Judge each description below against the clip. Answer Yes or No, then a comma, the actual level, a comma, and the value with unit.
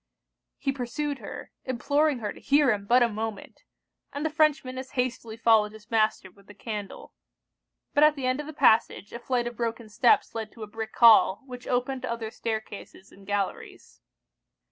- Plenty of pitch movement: No, average, 3.3 semitones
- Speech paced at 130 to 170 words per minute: No, average, 190 wpm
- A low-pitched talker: No, high, 235 Hz